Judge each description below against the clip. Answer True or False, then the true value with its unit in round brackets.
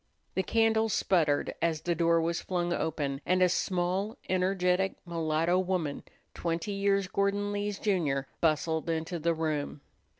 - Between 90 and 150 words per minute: True (140 wpm)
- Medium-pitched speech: True (175 Hz)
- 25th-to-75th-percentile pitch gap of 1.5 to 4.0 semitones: True (2.9 semitones)